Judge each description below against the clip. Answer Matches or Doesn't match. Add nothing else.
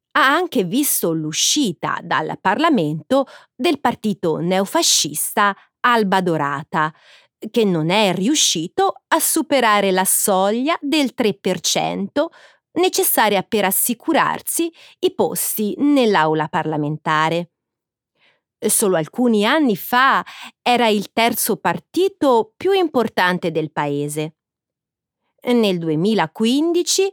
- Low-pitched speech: Doesn't match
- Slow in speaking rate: Matches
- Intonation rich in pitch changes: Matches